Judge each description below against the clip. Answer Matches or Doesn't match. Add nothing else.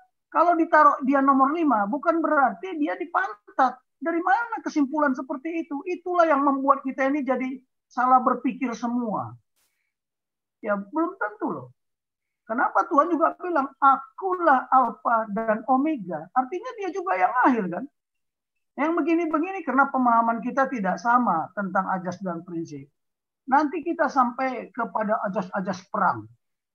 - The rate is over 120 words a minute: Matches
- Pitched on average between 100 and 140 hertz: Doesn't match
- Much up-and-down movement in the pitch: Matches